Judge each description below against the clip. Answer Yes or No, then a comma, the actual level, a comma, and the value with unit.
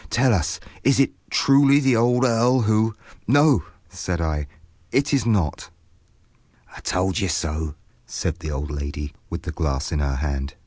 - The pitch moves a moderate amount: No, wide, 8.5 semitones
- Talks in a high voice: No, very low, 90 Hz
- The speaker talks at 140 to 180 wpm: Yes, average, 165 wpm